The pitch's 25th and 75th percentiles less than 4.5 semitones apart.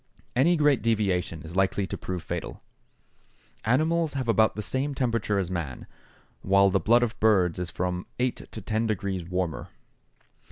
No: average, 5.1 semitones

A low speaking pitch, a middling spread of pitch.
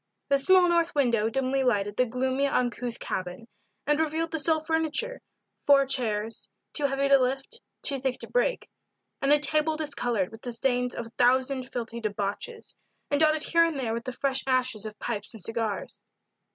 No: very high, 260 Hz; average, 4.3 semitones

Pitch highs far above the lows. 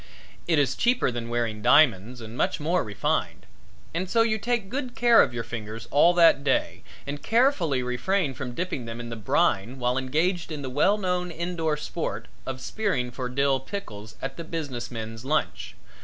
Yes: wide, 6.8 semitones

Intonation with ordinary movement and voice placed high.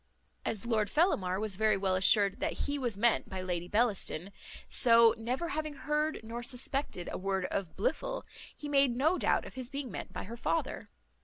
No: wide, 5.9 semitones; high, 230 Hz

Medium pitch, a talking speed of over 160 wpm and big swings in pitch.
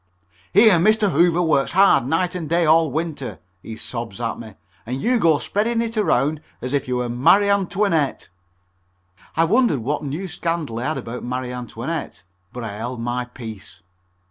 Yes: medium, 150 Hz; average, 170 wpm; wide, 6.3 semitones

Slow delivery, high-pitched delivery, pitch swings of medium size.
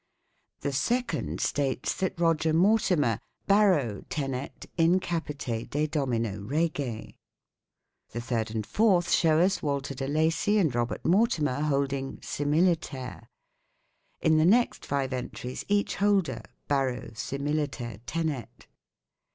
No: slow, 130 wpm; medium, 145 Hz; average, 4.7 semitones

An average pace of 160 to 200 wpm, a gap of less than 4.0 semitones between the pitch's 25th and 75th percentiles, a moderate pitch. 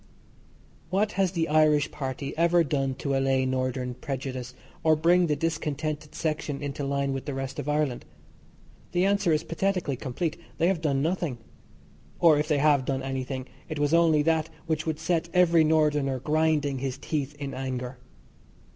Yes: average, 165 wpm; average, 3.2 semitones; medium, 150 Hz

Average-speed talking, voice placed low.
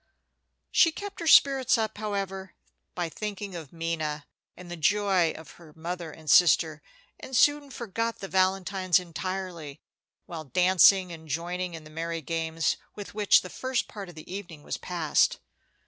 No: average, 160 wpm; medium, 180 Hz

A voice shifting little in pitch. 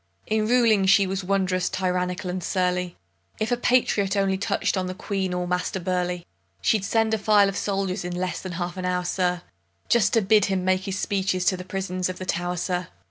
Yes: narrow, 1.7 semitones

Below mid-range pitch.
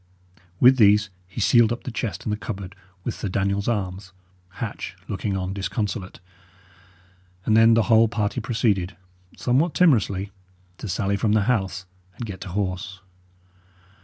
Yes: low, 105 Hz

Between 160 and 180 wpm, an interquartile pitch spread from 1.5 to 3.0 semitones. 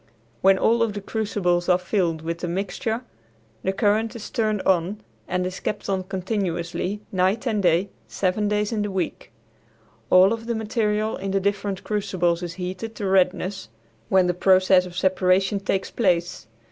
Yes: average, 170 wpm; narrow, 2.4 semitones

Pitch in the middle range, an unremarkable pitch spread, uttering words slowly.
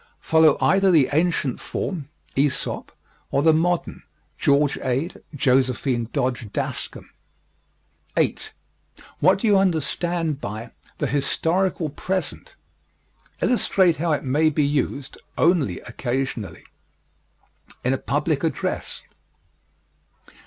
Yes: medium, 150 Hz; average, 4.4 semitones; slow, 105 wpm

